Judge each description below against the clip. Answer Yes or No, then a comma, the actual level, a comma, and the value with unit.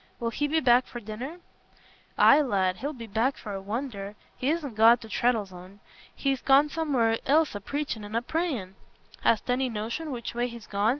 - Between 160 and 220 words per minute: Yes, average, 190 wpm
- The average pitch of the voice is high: Yes, high, 240 Hz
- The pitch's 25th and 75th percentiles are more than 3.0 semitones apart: Yes, average, 4.7 semitones